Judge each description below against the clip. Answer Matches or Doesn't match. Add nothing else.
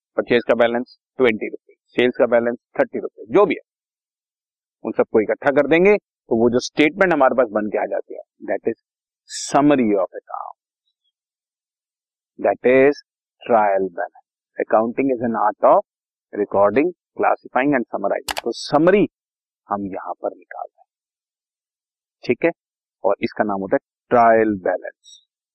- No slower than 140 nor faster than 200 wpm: Doesn't match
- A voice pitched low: Matches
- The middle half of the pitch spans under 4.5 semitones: Doesn't match